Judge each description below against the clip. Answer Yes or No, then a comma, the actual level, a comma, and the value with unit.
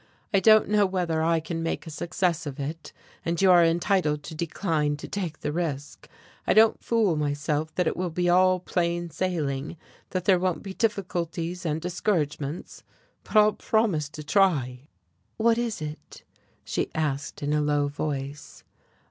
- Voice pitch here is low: No, medium, 170 Hz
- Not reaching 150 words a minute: No, average, 165 wpm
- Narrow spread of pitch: No, average, 3.6 semitones